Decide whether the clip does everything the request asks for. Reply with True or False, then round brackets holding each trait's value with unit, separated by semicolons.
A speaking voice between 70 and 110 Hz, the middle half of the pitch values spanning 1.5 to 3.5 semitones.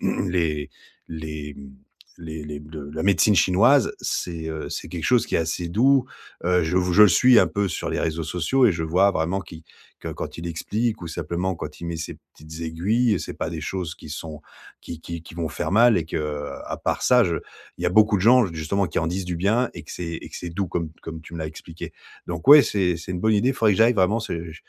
False (85 Hz; 4.1 semitones)